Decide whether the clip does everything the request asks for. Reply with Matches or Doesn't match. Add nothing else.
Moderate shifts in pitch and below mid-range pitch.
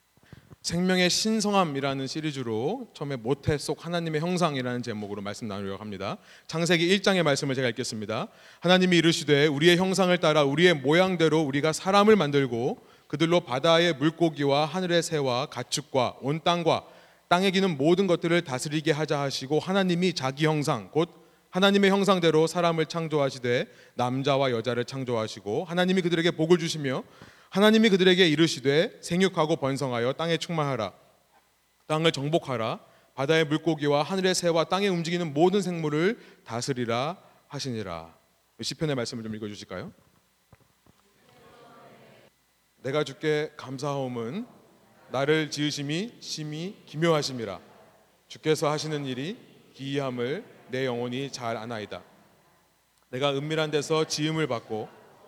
Doesn't match